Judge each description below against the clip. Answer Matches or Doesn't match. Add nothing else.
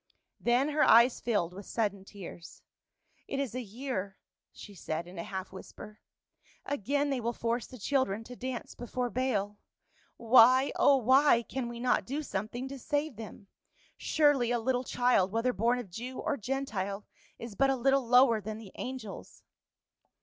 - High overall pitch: Matches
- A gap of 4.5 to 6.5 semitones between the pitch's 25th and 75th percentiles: Doesn't match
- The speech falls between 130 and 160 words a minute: Doesn't match